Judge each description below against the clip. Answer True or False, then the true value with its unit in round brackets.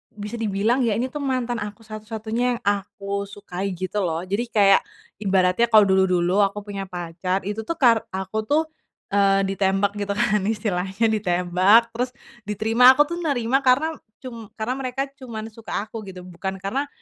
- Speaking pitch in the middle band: False (210 Hz)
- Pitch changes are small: False (3.3 semitones)